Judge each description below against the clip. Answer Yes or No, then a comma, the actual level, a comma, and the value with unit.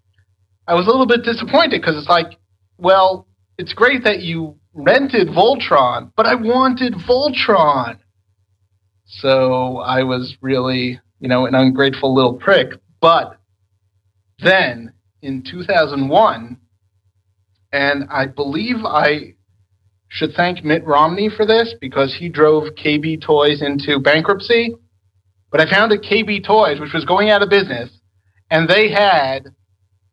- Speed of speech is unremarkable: No, slow, 130 wpm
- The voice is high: No, medium, 140 Hz